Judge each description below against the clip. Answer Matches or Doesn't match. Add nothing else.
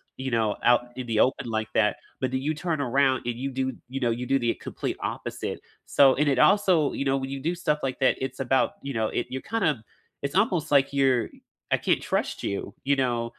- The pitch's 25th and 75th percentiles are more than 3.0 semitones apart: Doesn't match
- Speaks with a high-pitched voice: Doesn't match